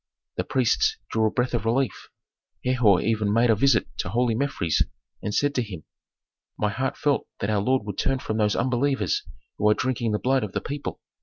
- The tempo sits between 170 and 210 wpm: Yes, fast, 205 wpm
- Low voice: Yes, low, 115 Hz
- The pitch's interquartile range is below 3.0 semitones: No, average, 3.6 semitones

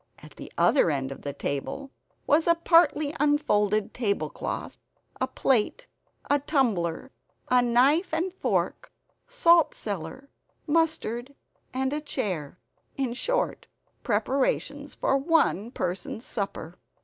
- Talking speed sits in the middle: No, slow, 115 wpm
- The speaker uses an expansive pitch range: Yes, wide, 6.6 semitones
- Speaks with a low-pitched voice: No, very high, 265 Hz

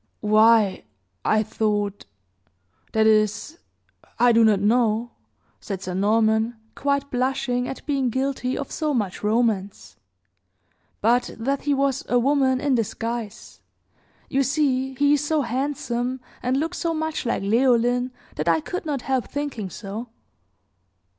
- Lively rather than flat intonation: No, average, 3.9 semitones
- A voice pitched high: Yes, high, 245 Hz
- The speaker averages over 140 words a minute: No, slow, 135 wpm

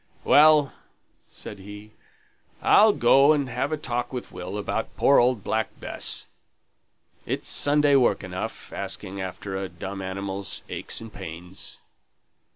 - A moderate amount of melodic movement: No, wide, 6.2 semitones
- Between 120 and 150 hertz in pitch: No, low, 110 Hz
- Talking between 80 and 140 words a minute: Yes, slow, 135 wpm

